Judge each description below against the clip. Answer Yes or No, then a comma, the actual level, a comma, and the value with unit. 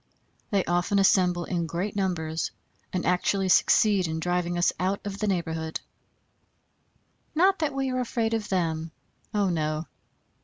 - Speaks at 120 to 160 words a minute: Yes, average, 145 wpm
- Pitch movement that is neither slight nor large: Yes, average, 3.3 semitones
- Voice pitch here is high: No, medium, 180 Hz